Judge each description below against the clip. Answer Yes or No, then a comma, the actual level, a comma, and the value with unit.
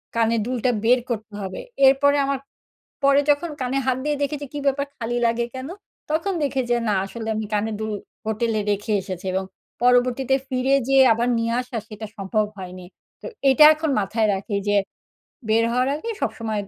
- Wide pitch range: No, average, 3.7 semitones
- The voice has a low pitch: No, high, 240 Hz